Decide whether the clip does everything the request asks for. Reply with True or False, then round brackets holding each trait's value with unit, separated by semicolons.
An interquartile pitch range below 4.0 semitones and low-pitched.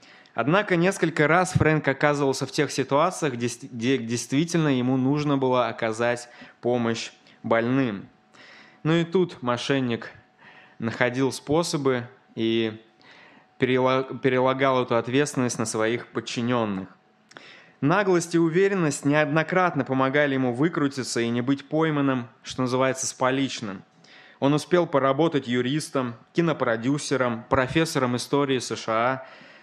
True (3.4 semitones; 130 Hz)